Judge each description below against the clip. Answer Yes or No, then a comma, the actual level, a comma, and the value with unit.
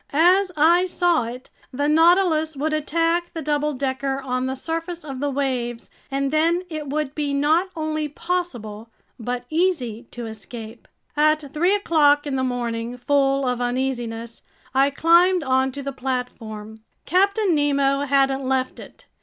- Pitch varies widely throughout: No, average, 4.0 semitones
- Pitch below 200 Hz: No, very high, 280 Hz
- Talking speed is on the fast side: No, average, 150 wpm